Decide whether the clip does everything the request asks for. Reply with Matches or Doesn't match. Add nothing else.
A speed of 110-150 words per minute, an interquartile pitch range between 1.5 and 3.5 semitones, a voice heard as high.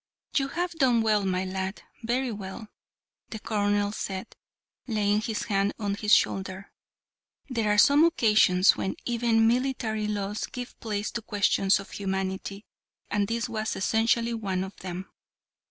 Matches